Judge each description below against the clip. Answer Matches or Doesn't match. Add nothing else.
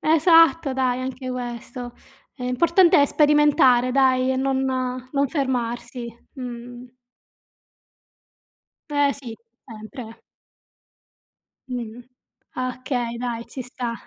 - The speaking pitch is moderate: Doesn't match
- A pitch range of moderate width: Doesn't match